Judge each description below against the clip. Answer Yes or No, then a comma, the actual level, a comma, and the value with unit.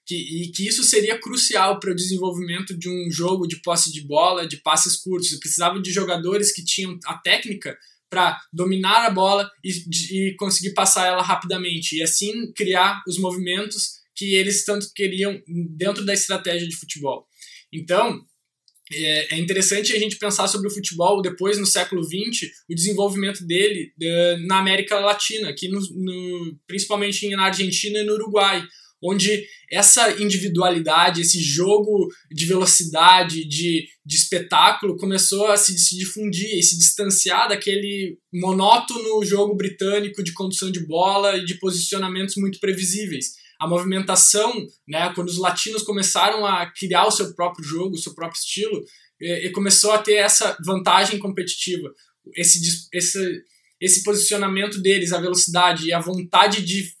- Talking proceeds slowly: No, average, 155 wpm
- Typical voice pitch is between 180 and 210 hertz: Yes, high, 190 Hz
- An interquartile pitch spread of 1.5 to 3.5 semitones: Yes, narrow, 2.4 semitones